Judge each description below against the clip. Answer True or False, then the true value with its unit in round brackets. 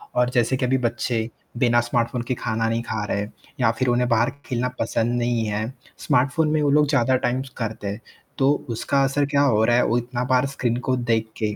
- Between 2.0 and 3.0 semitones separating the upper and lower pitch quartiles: True (2.4 semitones)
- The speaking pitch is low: True (120 Hz)